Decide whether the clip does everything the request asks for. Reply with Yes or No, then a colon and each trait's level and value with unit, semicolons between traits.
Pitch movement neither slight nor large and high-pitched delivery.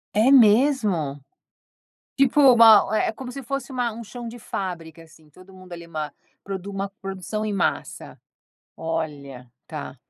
No: wide, 6.1 semitones; high, 195 Hz